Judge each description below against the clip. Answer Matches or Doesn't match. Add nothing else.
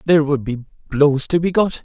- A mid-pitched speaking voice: Matches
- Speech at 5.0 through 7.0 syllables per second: Doesn't match